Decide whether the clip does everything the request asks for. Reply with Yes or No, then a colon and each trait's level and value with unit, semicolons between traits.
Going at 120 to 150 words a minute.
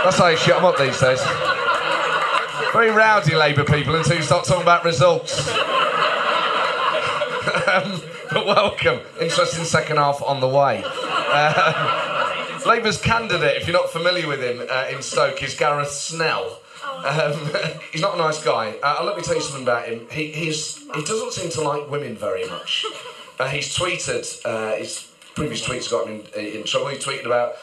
No: average, 175 wpm